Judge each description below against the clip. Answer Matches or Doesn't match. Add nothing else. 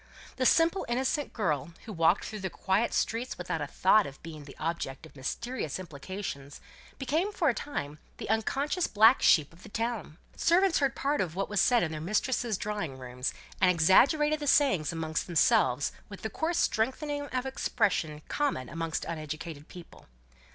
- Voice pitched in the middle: Doesn't match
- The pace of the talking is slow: Doesn't match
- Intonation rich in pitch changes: Matches